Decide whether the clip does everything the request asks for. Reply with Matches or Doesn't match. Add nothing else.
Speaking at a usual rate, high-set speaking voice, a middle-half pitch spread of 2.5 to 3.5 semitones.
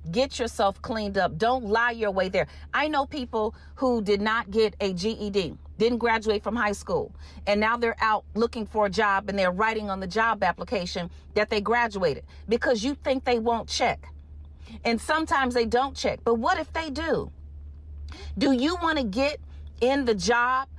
Doesn't match